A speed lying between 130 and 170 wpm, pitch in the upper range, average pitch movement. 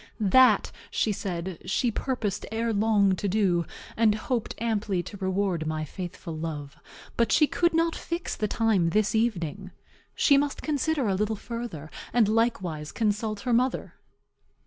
Yes: average, 150 wpm; high, 210 Hz; average, 4.1 semitones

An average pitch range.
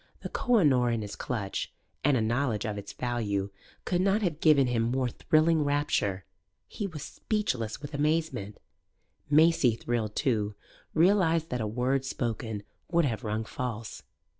No: wide, 6.1 semitones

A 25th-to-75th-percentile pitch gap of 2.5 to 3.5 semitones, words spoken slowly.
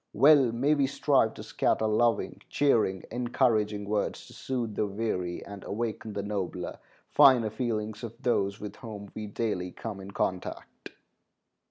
No: average, 2.8 semitones; average, 150 wpm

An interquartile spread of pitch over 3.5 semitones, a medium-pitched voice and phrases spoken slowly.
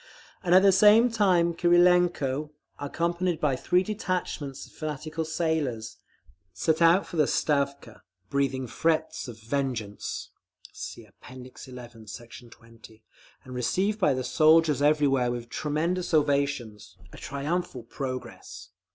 Yes: average, 5.3 semitones; medium, 145 Hz; slow, 120 wpm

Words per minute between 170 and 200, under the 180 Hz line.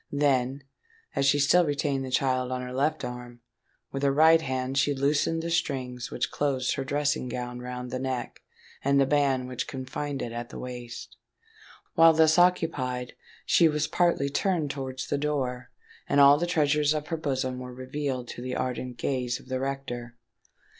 Yes: average, 180 wpm; low, 135 Hz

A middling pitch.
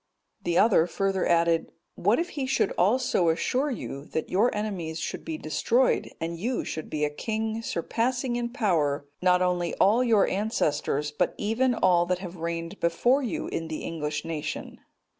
Yes: medium, 180 Hz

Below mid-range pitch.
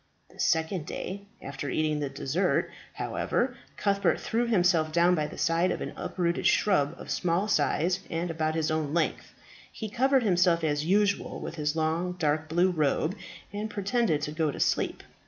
No: medium, 170 Hz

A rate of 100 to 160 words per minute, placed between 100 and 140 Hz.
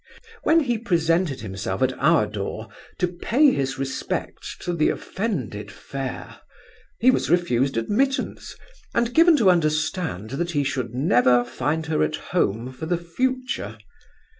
No: average, 140 wpm; medium, 155 Hz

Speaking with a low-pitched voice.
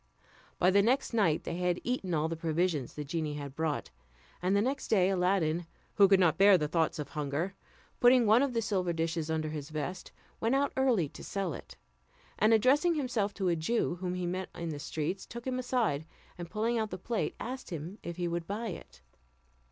No: medium, 180 Hz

